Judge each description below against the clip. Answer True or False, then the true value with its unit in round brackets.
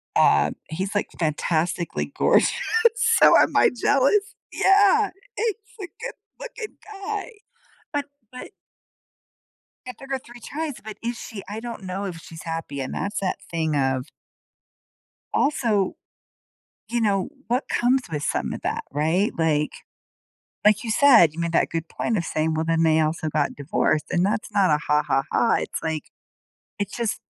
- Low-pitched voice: False (195 Hz)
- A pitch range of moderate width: False (7.5 semitones)